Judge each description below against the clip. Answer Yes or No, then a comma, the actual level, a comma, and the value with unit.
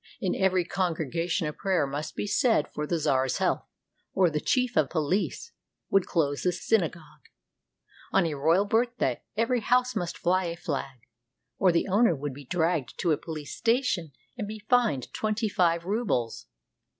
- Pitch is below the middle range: No, medium, 175 Hz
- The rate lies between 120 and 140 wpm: No, average, 165 wpm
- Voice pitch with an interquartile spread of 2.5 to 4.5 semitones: No, wide, 5.4 semitones